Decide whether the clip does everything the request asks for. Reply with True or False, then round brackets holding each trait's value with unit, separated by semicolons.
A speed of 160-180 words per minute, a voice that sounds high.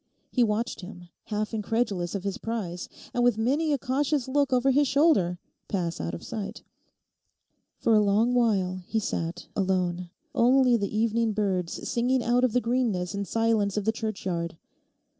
True (165 wpm; 220 Hz)